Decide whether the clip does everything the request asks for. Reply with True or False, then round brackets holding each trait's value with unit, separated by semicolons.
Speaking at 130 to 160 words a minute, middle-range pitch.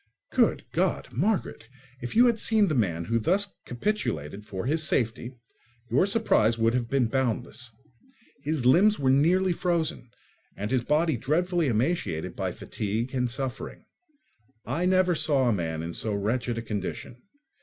False (155 wpm; 130 Hz)